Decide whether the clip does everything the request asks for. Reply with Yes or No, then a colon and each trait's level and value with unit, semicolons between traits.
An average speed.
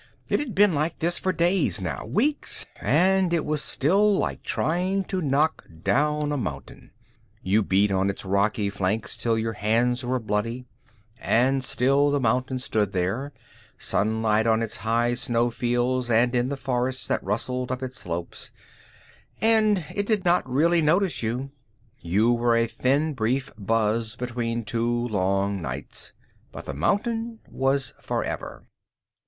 Yes: average, 150 wpm